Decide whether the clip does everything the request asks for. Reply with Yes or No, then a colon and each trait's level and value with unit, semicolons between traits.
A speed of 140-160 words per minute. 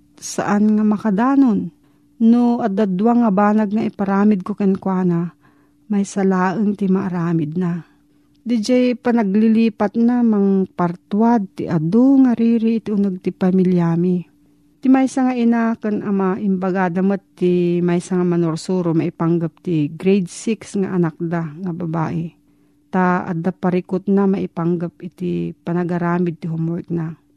No: average, 130 wpm